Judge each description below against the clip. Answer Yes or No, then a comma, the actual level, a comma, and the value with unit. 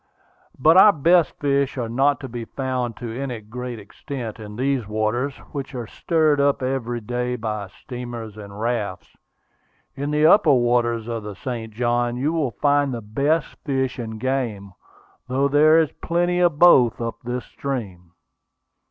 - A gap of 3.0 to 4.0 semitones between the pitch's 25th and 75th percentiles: Yes, average, 3.6 semitones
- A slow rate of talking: No, average, 160 wpm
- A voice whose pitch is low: Yes, low, 125 Hz